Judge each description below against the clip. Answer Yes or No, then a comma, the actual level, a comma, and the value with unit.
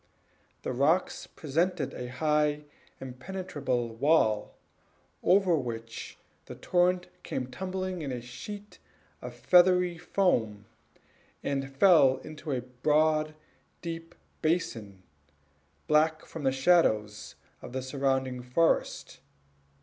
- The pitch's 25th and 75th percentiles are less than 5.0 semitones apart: No, average, 5.3 semitones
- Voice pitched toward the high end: No, medium, 150 Hz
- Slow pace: Yes, slow, 105 wpm